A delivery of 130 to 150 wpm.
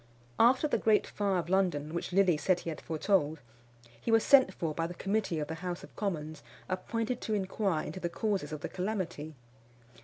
No: average, 195 wpm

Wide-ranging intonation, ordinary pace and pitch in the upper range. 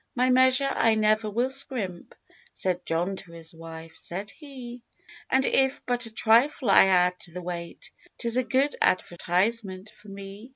Yes: wide, 5.7 semitones; average, 165 wpm; high, 215 Hz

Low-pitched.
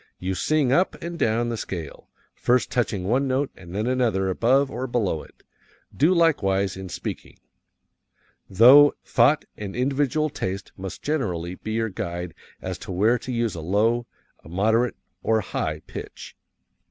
Yes: low, 115 Hz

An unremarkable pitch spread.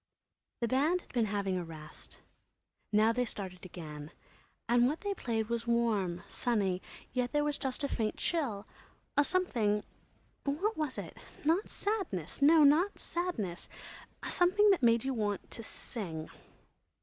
No: wide, 6.8 semitones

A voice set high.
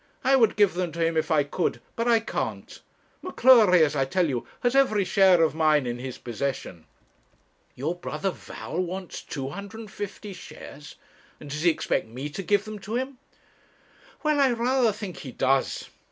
No: medium, 180 Hz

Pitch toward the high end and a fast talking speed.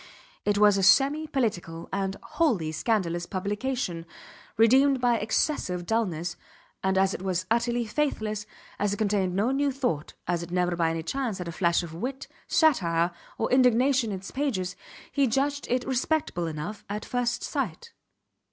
No: high, 210 Hz; average, 160 wpm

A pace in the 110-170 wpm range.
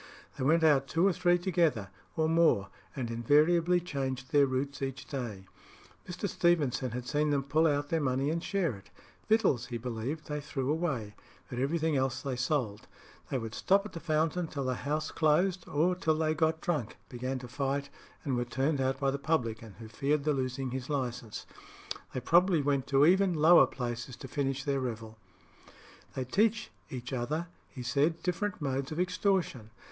No: average, 180 wpm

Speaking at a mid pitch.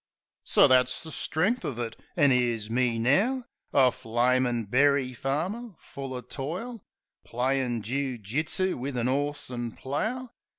No: low, 130 Hz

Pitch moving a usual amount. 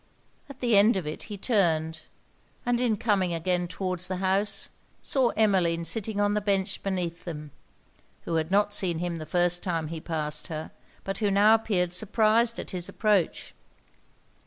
Yes: average, 3.7 semitones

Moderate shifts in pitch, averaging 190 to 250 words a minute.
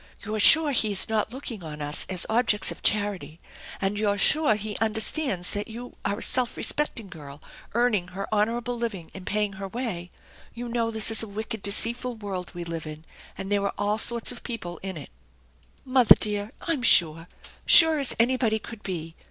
Yes: average, 3.8 semitones; average, 195 wpm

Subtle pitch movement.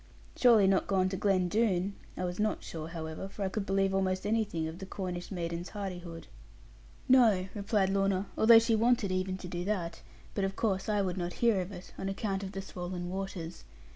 Yes: narrow, 2.2 semitones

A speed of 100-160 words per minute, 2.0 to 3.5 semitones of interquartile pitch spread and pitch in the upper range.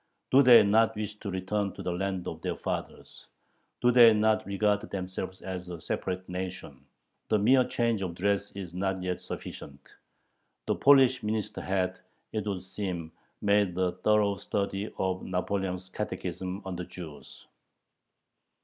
No: average, 150 wpm; narrow, 2.5 semitones; very low, 95 Hz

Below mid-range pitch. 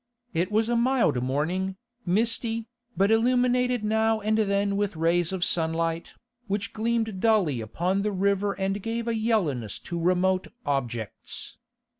No: high, 200 Hz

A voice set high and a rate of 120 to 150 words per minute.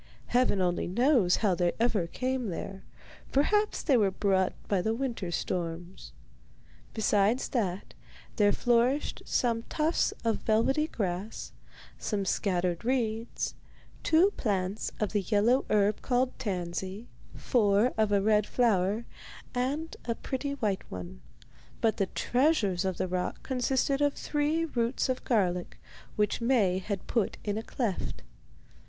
Yes: high, 215 Hz; slow, 135 wpm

